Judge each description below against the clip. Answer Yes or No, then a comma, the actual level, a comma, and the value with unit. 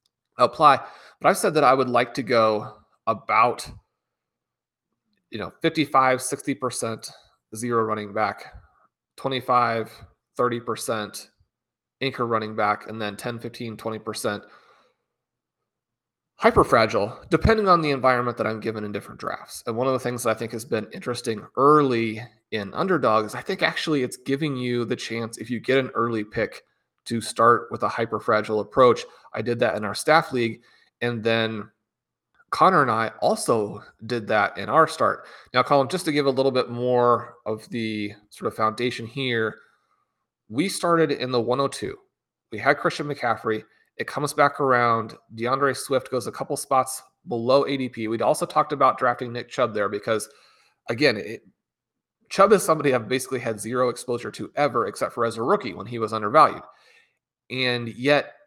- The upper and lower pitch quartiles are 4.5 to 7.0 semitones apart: No, average, 3.2 semitones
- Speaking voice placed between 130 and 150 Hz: No, low, 120 Hz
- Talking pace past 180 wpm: No, average, 170 wpm